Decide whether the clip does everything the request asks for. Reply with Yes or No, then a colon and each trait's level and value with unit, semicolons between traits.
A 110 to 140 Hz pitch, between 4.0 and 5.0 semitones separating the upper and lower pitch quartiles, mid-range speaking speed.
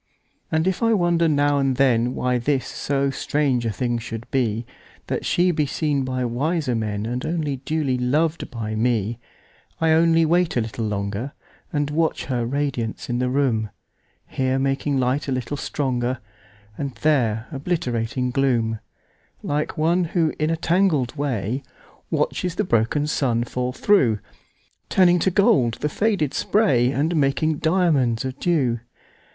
No: low, 135 Hz; average, 4.7 semitones; slow, 130 wpm